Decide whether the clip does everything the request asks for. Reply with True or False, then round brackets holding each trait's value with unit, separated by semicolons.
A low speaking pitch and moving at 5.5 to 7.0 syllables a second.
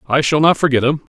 False (145 Hz; 6.4 syllables/s)